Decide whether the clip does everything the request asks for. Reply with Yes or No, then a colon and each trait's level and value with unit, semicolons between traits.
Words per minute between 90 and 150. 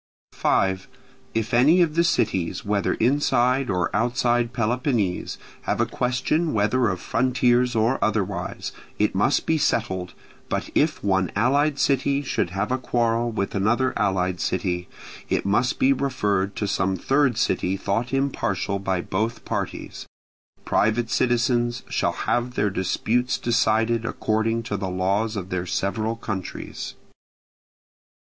Yes: slow, 135 wpm